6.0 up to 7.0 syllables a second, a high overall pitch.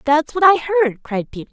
Yes: 6.9 syllables/s; very high, 295 Hz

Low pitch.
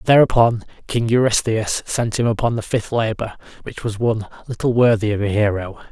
Yes: low, 110 Hz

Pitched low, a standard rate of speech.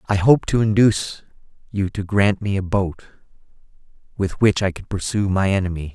Yes: low, 100 Hz; average, 170 wpm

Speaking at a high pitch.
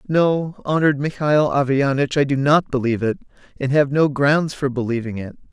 No: medium, 140 Hz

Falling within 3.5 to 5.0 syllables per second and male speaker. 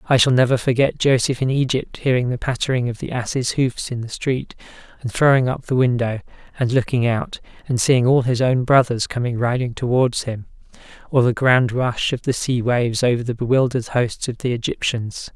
No: 5.3 syllables/s; male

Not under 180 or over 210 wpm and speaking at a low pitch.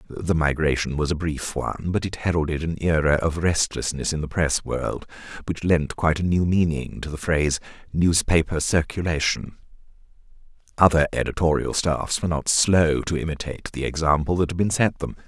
No: average, 170 wpm; very low, 80 Hz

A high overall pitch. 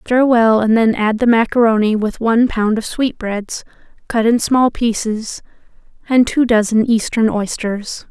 Yes: high, 225 Hz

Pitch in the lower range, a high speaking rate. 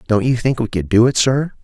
Yes: low, 120 Hz; fast, 295 wpm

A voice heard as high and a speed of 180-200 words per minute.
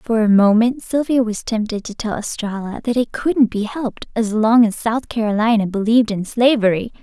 Yes: high, 225 Hz; average, 190 wpm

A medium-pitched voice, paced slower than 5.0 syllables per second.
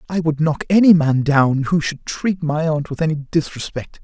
Yes: medium, 155 Hz; 4.7 syllables/s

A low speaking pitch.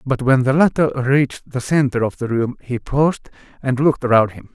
Yes: low, 130 Hz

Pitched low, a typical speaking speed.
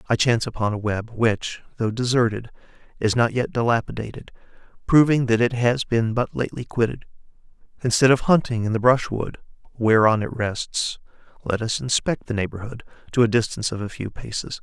Yes: low, 115 Hz; average, 170 wpm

